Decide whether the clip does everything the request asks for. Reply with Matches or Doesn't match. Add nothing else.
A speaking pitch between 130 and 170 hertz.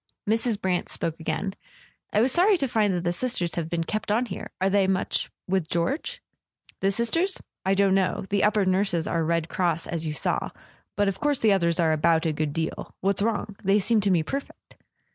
Doesn't match